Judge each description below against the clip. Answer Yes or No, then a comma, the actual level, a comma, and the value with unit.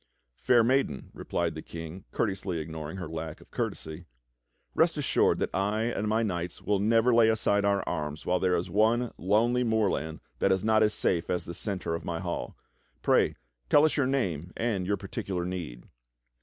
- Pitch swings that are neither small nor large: Yes, average, 4.6 semitones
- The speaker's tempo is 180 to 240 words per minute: Yes, average, 185 wpm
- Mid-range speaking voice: No, very low, 95 Hz